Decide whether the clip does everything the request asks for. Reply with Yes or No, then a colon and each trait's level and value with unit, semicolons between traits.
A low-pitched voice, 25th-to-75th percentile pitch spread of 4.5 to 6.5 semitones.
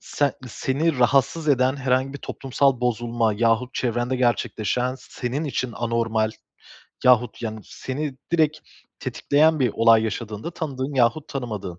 No: low, 125 Hz; average, 3.0 semitones